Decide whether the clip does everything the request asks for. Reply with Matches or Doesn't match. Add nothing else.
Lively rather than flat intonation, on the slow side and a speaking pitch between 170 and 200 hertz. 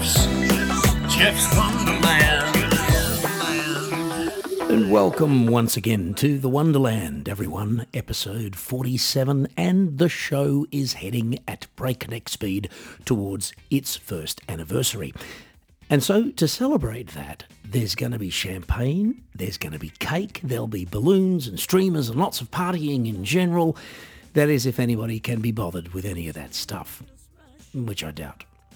Doesn't match